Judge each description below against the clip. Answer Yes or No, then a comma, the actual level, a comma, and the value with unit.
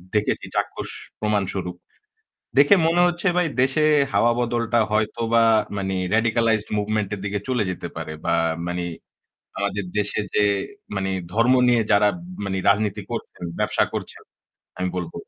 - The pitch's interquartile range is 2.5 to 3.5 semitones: Yes, average, 2.9 semitones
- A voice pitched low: Yes, low, 105 Hz